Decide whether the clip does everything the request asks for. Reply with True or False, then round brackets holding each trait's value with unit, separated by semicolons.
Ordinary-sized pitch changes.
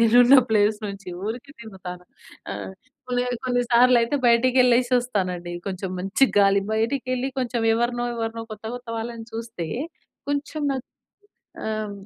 True (3.0 semitones)